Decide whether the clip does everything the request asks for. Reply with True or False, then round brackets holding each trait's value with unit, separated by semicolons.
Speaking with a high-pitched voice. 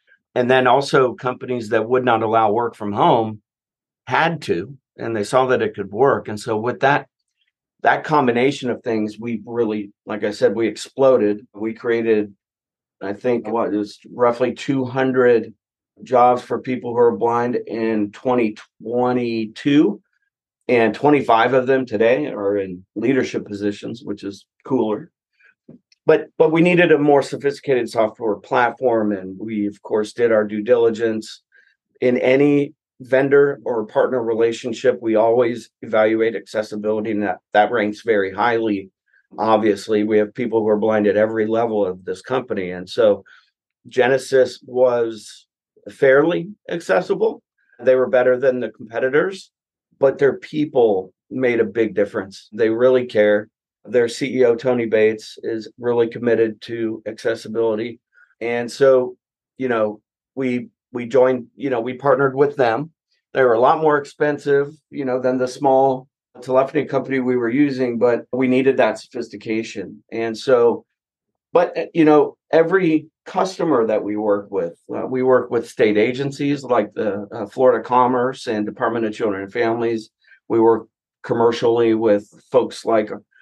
False (120 Hz)